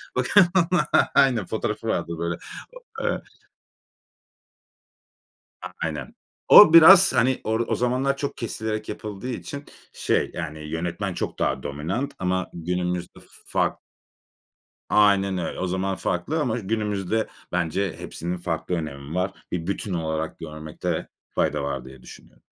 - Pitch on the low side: Yes, very low, 95 Hz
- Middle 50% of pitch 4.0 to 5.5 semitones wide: Yes, average, 5.1 semitones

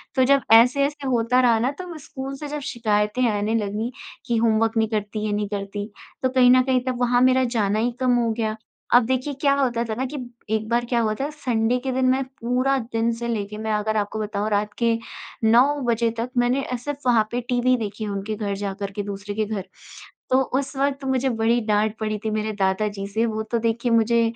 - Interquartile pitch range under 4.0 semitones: Yes, average, 3.0 semitones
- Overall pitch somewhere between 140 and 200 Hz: No, high, 230 Hz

